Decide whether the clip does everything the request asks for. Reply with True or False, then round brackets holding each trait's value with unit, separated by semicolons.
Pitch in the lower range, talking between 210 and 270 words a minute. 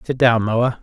True (120 Hz; 220 wpm)